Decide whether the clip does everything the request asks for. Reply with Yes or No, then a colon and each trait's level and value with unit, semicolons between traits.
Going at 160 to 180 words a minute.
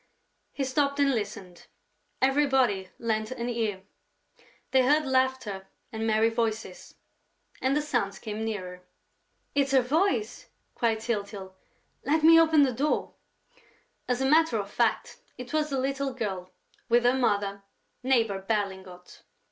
No: slow, 135 wpm